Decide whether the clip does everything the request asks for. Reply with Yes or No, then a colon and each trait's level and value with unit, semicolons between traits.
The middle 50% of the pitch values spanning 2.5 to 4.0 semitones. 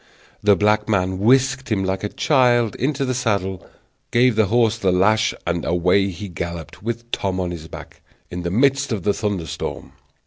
No: average, 4.4 semitones